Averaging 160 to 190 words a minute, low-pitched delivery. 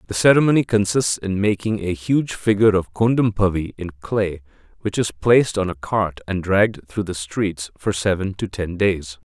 Yes: average, 180 wpm; very low, 95 Hz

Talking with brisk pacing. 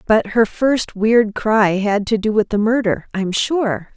No: average, 195 wpm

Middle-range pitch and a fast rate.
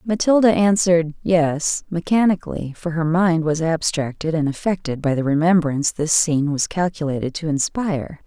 No: medium, 165 Hz; average, 145 wpm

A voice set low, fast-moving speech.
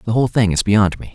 Yes: low, 105 Hz; fast, 315 wpm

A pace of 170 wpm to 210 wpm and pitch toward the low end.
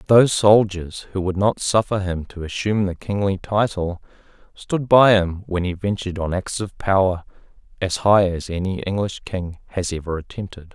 Yes: average, 175 wpm; very low, 95 Hz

